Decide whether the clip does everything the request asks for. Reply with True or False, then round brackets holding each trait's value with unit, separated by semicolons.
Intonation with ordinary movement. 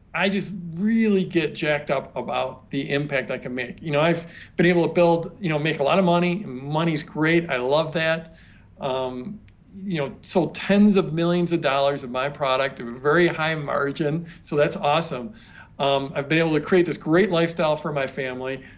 True (3.8 semitones)